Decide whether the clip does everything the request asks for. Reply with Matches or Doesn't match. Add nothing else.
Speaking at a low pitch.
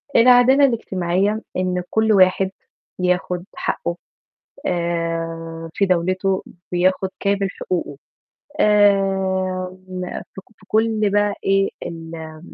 Doesn't match